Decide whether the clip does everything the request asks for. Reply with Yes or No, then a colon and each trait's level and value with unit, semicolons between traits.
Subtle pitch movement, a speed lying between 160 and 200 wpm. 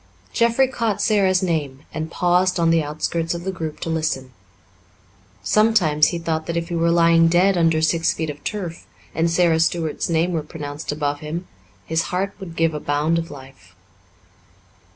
Yes: narrow, 2.2 semitones; average, 175 wpm